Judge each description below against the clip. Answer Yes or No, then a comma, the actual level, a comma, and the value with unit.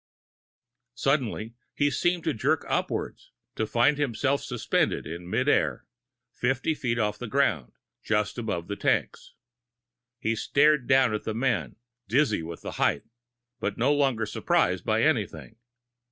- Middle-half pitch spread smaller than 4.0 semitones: No, average, 4.5 semitones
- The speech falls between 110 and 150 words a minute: Yes, average, 140 wpm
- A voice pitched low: Yes, low, 120 Hz